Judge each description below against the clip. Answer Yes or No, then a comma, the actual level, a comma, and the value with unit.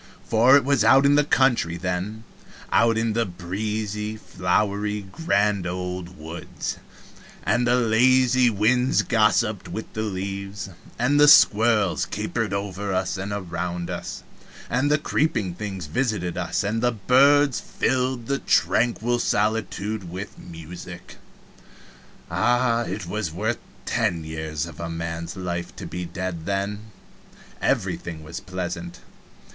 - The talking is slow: Yes, slow, 130 wpm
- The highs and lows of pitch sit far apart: No, average, 4.7 semitones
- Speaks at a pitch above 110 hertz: No, low, 105 Hz